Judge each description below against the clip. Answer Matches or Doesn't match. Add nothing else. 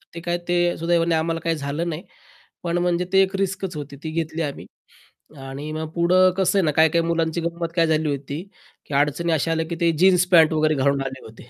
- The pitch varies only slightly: Matches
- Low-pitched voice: Doesn't match